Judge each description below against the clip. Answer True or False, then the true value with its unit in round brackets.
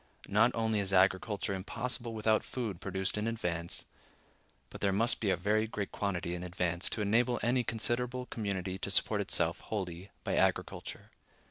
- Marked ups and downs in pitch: False (3.3 semitones)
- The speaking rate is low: False (160 wpm)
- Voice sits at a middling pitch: False (105 Hz)